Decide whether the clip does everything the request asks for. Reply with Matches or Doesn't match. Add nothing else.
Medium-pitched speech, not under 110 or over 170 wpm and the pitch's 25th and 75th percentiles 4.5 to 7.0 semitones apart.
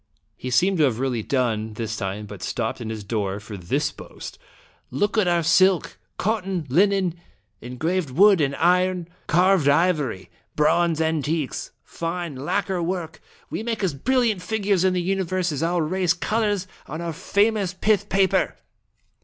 Matches